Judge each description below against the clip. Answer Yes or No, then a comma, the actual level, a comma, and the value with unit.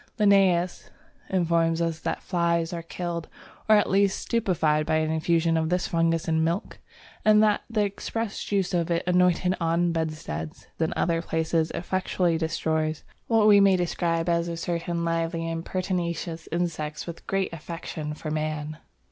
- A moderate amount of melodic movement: No, narrow, 1.9 semitones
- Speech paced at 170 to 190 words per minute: No, average, 155 wpm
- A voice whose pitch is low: No, medium, 170 Hz